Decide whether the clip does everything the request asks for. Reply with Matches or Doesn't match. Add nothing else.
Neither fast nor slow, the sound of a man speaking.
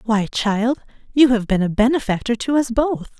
Doesn't match